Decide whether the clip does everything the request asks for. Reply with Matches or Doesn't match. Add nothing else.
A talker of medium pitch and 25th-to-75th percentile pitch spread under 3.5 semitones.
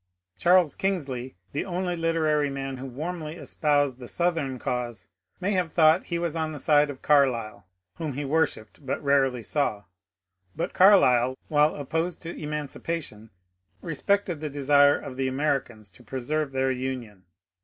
Doesn't match